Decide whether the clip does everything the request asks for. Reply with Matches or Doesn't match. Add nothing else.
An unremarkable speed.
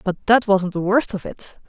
Doesn't match